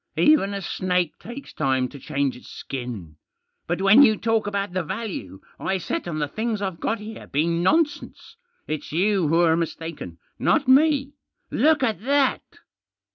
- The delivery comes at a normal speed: Yes, average, 160 wpm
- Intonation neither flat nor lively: No, wide, 6.8 semitones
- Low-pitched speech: No, high, 190 Hz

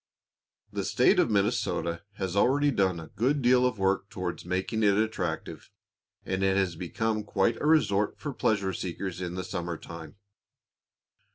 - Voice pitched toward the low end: Yes, very low, 95 Hz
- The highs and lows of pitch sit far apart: No, average, 3.8 semitones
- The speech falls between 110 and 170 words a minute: Yes, average, 160 wpm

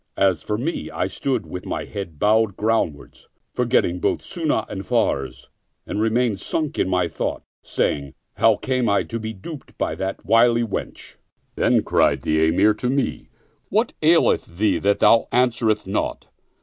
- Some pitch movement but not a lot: Yes, average, 4.0 semitones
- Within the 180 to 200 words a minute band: No, average, 165 wpm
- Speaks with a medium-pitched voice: No, low, 110 Hz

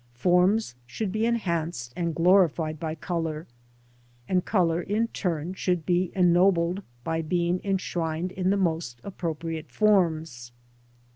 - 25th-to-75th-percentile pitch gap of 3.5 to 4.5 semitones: No, narrow, 2.5 semitones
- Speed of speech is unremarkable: No, slow, 125 wpm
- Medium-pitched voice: Yes, medium, 175 Hz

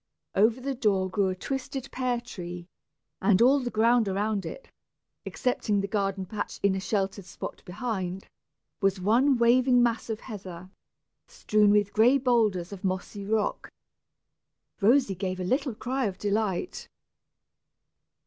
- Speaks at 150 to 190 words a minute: No, average, 140 wpm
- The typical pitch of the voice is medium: No, high, 210 Hz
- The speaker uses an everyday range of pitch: Yes, average, 4.1 semitones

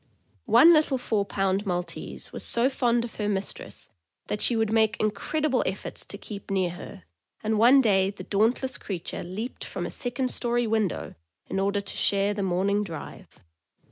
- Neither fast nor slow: Yes, average, 175 wpm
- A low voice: No, high, 210 Hz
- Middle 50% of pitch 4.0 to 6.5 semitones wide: No, average, 3.5 semitones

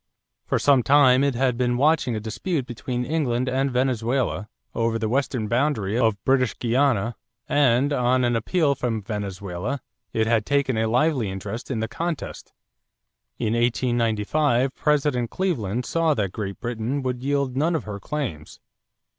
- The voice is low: Yes, low, 125 Hz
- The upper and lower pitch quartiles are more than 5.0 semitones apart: No, average, 3.8 semitones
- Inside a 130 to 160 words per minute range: Yes, average, 155 wpm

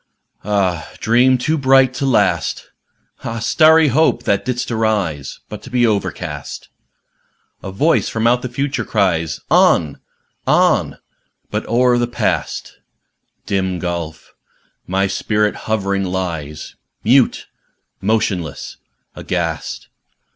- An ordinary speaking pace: No, slow, 110 wpm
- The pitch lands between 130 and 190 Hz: No, low, 110 Hz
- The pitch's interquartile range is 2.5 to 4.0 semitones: No, average, 5.0 semitones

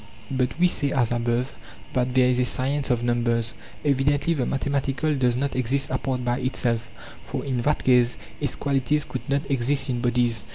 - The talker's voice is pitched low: Yes, low, 130 Hz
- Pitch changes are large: No, narrow, 2.4 semitones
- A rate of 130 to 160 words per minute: No, average, 190 wpm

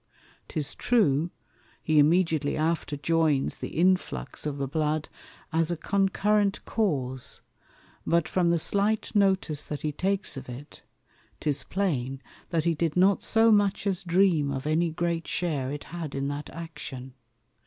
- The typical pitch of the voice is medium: Yes, medium, 165 Hz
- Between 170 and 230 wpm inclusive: No, average, 150 wpm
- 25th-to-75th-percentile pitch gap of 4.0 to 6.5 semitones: Yes, average, 4.4 semitones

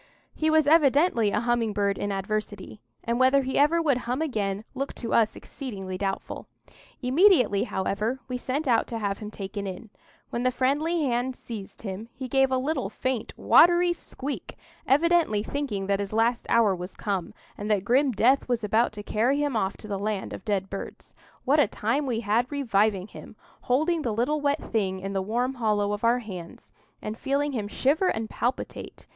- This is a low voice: No, high, 235 Hz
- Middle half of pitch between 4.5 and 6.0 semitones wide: Yes, average, 4.9 semitones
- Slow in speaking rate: No, average, 185 wpm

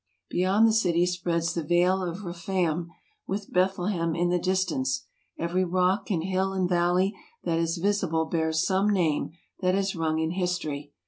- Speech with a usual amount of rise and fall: No, narrow, 2.2 semitones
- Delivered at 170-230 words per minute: No, average, 160 wpm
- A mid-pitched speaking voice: Yes, medium, 180 Hz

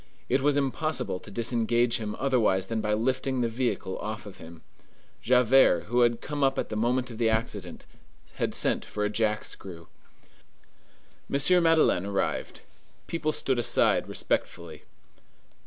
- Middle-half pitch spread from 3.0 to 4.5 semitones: Yes, average, 3.9 semitones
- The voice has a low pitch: Yes, low, 120 Hz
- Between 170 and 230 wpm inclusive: No, average, 150 wpm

